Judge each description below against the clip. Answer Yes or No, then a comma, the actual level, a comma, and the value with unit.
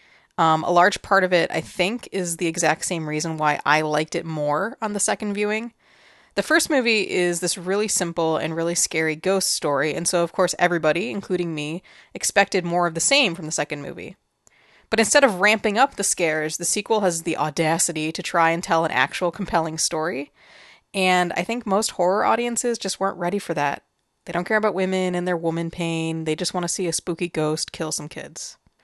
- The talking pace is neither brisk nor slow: No, fast, 210 wpm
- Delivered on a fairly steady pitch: No, average, 3.3 semitones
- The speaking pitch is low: No, medium, 175 Hz